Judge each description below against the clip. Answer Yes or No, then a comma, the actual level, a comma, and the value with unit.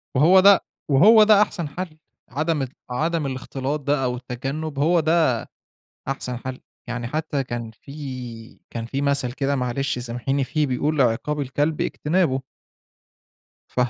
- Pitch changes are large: No, average, 3.7 semitones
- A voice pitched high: No, medium, 140 Hz